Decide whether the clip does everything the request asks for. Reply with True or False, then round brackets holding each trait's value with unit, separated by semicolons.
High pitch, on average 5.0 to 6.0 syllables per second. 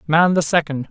False (160 Hz; 5.2 syllables/s)